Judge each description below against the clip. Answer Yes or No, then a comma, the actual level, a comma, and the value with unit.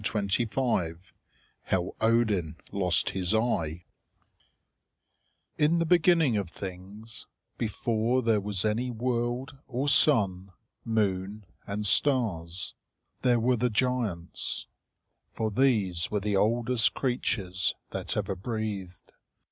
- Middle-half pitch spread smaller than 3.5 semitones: No, average, 4.2 semitones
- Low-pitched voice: Yes, low, 110 Hz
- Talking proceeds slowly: Yes, slow, 110 wpm